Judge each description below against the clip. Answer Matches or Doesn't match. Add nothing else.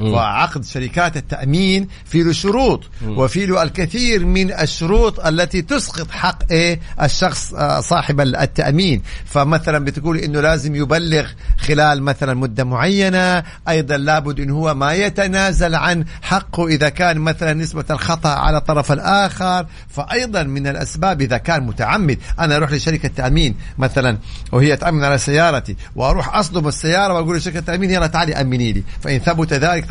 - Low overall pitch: Doesn't match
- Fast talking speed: Doesn't match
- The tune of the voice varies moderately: Matches